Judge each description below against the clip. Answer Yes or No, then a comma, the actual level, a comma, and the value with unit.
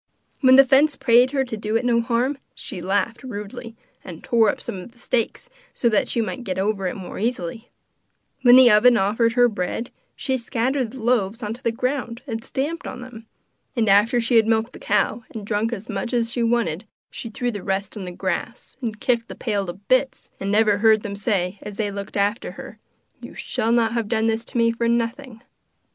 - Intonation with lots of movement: No, average, 2.9 semitones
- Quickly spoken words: Yes, fast, 215 wpm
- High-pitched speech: Yes, high, 230 Hz